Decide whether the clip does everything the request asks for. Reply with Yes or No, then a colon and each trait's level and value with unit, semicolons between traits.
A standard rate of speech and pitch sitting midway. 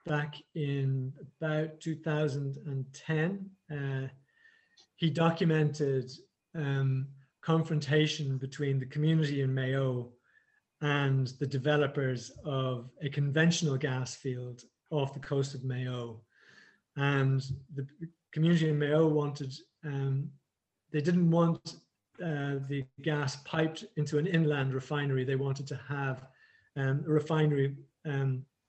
No: slow, 110 wpm; medium, 145 Hz